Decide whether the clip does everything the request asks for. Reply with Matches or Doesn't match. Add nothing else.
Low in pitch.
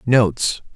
Matches